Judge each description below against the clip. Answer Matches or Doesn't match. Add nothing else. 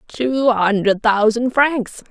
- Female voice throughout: Matches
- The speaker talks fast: Doesn't match